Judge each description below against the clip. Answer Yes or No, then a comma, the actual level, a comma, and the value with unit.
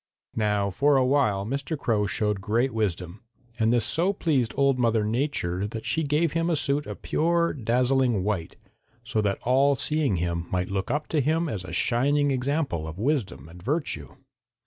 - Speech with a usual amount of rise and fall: No, wide, 5.9 semitones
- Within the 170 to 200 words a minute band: Yes, average, 180 wpm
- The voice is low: Yes, low, 120 Hz